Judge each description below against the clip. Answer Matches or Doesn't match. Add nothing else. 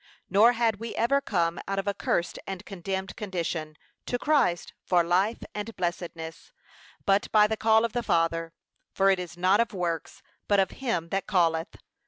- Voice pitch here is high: Matches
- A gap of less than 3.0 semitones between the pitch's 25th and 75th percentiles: Doesn't match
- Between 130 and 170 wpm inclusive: Doesn't match